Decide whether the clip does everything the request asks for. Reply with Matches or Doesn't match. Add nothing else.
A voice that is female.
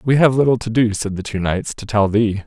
Doesn't match